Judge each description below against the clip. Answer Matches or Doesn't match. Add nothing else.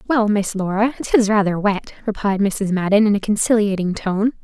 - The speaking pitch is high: Matches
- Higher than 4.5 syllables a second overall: Matches